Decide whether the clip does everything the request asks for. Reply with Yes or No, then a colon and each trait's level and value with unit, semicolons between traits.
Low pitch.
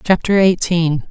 No: medium, 175 Hz